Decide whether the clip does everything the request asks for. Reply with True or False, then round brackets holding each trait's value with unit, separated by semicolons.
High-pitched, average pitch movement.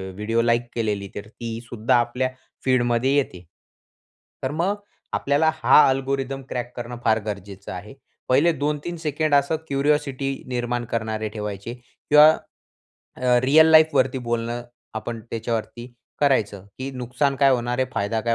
False (125 Hz; 3.4 semitones)